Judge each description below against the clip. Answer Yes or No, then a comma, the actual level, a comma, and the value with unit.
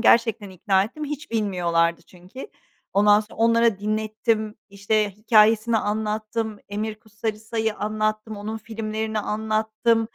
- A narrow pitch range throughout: Yes, narrow, 1.2 semitones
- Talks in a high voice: Yes, high, 215 Hz